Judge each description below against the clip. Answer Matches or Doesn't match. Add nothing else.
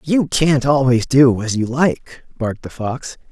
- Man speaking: Matches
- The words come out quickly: Doesn't match